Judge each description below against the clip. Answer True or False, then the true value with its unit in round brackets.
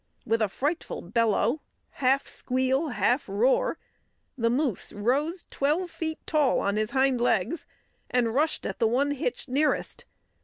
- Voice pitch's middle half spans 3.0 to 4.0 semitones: False (4.5 semitones)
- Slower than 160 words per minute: True (145 wpm)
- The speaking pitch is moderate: False (260 Hz)